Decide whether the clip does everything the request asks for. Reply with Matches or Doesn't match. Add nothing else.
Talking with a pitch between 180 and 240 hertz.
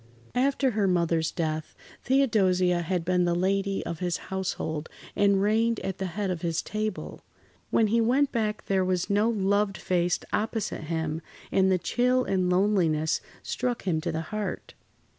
Matches